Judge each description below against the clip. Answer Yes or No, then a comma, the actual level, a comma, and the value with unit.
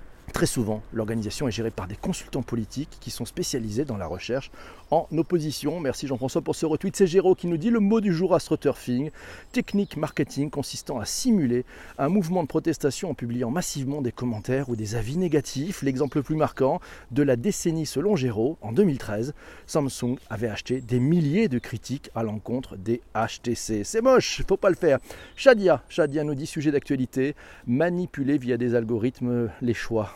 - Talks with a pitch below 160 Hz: Yes, medium, 140 Hz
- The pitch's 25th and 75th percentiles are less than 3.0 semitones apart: No, wide, 5.4 semitones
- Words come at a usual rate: Yes, average, 180 wpm